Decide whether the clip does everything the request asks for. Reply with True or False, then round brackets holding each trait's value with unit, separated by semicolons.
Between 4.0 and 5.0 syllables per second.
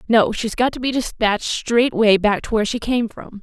False (5.2 syllables/s)